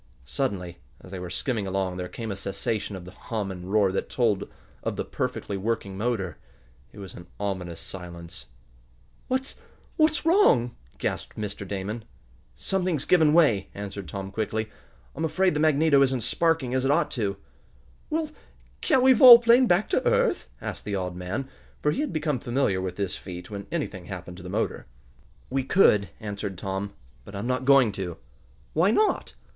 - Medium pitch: No, low, 105 Hz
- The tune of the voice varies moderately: No, wide, 7.6 semitones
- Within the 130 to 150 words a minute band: No, average, 175 wpm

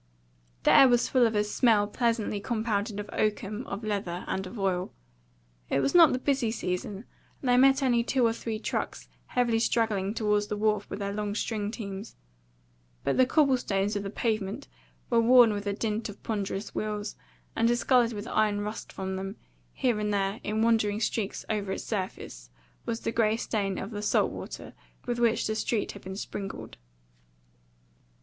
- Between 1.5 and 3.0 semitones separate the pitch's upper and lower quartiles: Yes, narrow, 2.4 semitones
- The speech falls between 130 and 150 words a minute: No, average, 185 wpm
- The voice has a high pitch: Yes, high, 215 Hz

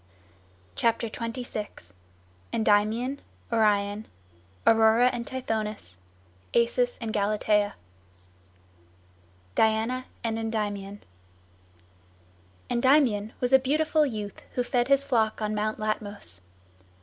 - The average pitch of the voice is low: No, high, 225 Hz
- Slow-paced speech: Yes, slow, 90 wpm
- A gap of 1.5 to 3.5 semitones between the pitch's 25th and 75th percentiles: Yes, average, 2.8 semitones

